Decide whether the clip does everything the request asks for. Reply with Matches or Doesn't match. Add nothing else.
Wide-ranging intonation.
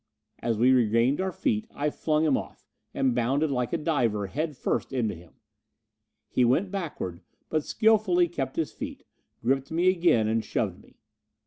Matches